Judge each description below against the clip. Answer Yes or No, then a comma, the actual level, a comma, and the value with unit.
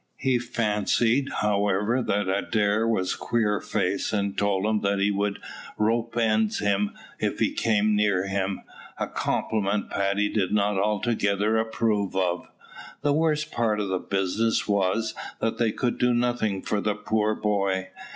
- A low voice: Yes, low, 105 Hz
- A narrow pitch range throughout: Yes, narrow, 2.1 semitones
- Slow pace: No, average, 150 wpm